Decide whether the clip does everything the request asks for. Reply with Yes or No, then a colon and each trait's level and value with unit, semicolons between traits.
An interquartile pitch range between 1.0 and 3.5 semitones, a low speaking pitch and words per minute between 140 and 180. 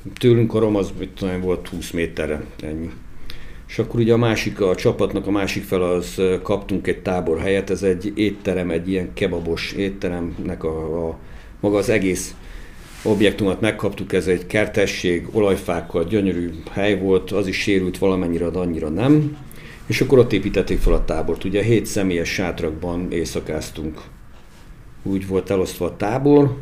Yes: narrow, 2.6 semitones; very low, 95 Hz; fast, 155 wpm